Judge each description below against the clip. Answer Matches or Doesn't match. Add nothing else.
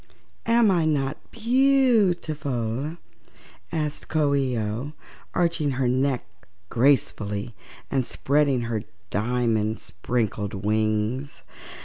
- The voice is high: Doesn't match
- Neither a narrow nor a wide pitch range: Doesn't match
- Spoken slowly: Matches